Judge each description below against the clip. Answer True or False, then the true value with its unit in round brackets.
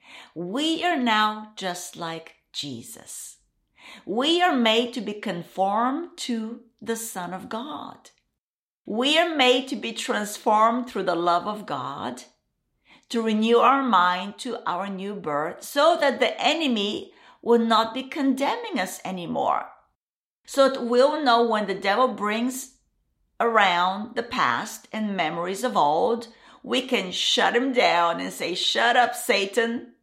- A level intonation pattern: False (4.5 semitones)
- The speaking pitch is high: True (230 Hz)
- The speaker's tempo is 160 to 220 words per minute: False (140 wpm)